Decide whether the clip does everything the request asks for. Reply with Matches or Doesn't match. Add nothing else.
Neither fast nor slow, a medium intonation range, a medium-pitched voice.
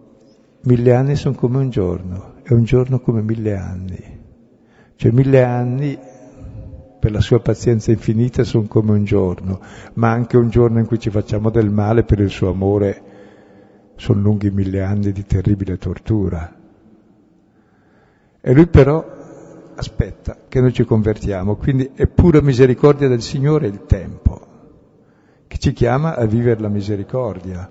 Doesn't match